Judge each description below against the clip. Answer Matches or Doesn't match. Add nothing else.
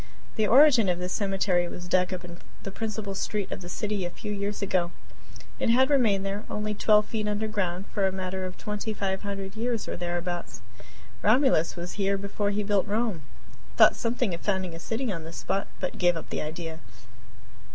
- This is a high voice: Matches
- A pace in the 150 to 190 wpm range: Doesn't match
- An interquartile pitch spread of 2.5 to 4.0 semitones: Matches